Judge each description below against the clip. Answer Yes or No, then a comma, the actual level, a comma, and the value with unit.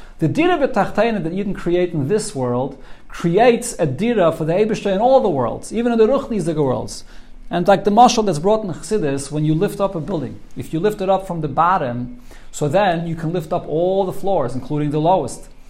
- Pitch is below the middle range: No, medium, 180 Hz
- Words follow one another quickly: Yes, fast, 230 wpm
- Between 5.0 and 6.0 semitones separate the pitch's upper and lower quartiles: Yes, wide, 5.5 semitones